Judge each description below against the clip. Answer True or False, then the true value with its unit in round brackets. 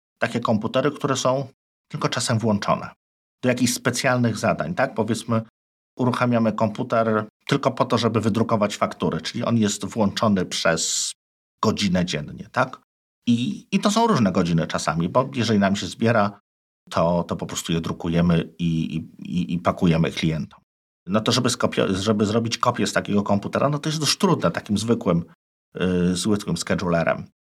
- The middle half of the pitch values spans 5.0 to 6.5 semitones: True (5.4 semitones)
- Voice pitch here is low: True (110 Hz)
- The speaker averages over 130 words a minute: True (155 wpm)